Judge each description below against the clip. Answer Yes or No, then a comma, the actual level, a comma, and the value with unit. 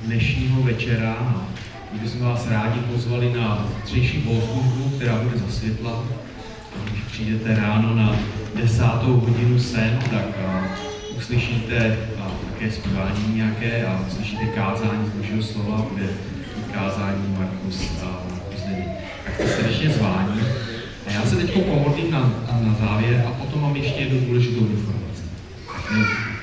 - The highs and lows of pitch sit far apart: No, narrow, 2.4 semitones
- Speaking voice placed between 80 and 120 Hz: Yes, low, 110 Hz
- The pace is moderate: Yes, average, 125 wpm